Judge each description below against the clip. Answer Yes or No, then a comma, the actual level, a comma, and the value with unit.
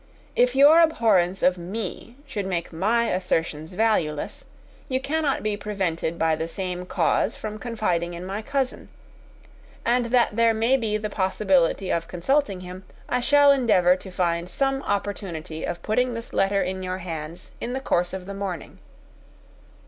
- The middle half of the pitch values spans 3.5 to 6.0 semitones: Yes, average, 4.8 semitones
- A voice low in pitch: No, high, 195 Hz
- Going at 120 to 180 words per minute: Yes, average, 160 wpm